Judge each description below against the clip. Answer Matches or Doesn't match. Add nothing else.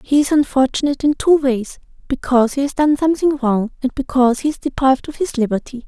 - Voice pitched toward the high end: Matches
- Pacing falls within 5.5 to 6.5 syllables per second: Matches